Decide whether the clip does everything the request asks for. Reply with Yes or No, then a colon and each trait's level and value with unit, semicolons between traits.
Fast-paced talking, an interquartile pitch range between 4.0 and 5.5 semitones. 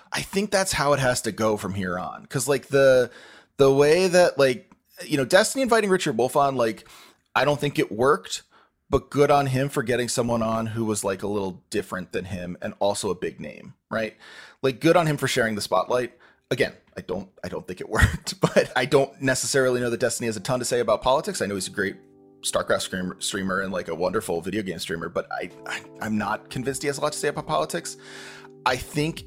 Yes: fast, 235 wpm; average, 4.5 semitones